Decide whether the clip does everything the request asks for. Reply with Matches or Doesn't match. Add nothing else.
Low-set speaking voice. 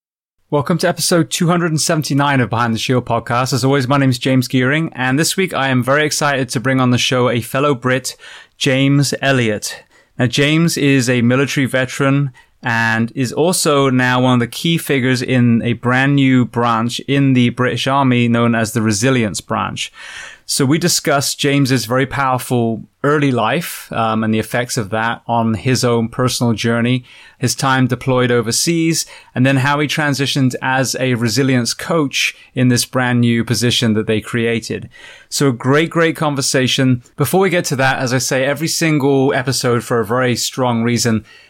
Matches